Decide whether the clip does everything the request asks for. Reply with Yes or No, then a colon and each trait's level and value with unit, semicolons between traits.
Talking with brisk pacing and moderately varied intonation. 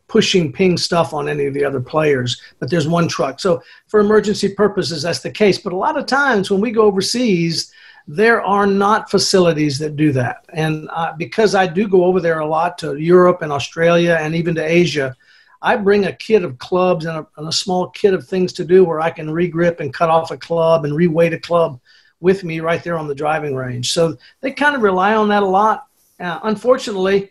Yes: fast, 225 wpm; average, 3.8 semitones